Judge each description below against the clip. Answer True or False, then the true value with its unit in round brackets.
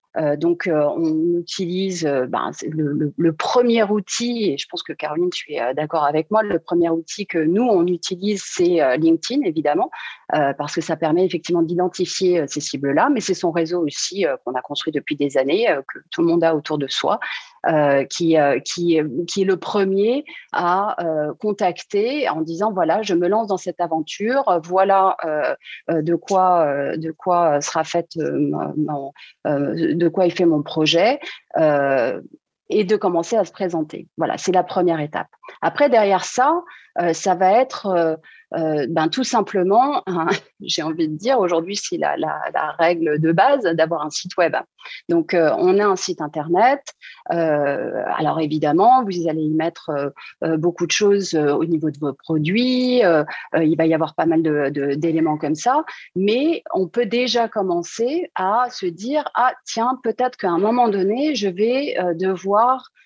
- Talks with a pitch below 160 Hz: False (175 Hz)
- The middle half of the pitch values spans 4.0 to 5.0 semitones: True (4.7 semitones)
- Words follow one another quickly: False (190 wpm)